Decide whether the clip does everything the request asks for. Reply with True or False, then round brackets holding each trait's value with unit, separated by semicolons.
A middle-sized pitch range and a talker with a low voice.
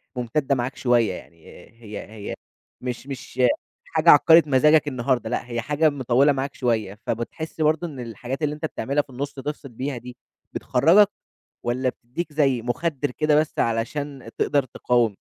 True (3.7 semitones; 130 Hz)